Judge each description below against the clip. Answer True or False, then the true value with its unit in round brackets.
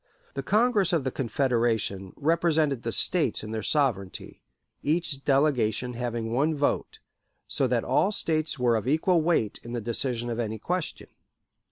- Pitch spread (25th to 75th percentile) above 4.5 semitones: True (5.2 semitones)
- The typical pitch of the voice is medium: False (130 Hz)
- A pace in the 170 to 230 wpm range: False (160 wpm)